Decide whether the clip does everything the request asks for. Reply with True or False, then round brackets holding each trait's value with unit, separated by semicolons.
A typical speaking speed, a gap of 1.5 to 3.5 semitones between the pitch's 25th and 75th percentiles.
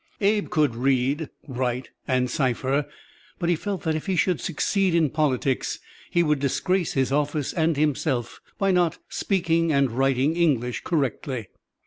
False (150 wpm; 4.4 semitones)